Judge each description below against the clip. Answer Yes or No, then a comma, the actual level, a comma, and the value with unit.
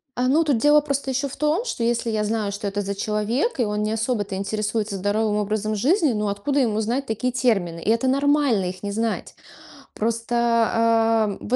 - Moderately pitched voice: No, high, 225 Hz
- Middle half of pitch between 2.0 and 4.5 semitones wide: Yes, average, 3.5 semitones